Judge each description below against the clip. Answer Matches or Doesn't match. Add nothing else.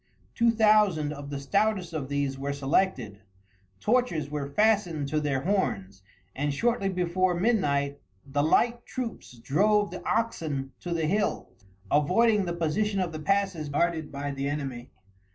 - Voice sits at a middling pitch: Matches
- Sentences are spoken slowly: Doesn't match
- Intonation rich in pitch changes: Matches